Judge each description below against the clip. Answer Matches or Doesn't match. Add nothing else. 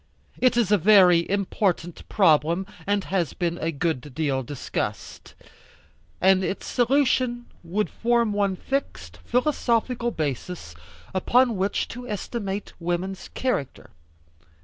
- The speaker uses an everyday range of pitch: Doesn't match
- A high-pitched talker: Matches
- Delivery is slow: Matches